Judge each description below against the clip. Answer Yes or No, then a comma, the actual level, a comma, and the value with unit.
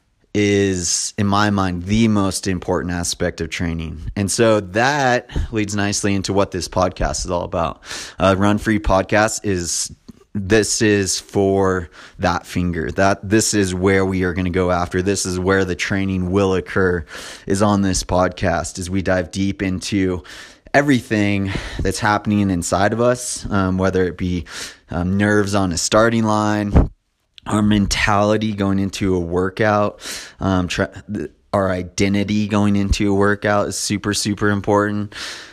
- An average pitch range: No, narrow, 2.2 semitones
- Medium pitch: No, low, 100 Hz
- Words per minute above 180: No, average, 155 wpm